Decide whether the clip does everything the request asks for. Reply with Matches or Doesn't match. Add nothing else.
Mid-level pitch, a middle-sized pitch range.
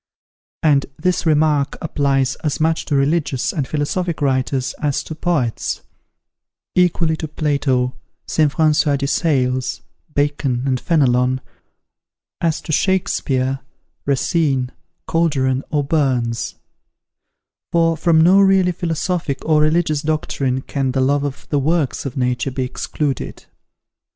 Matches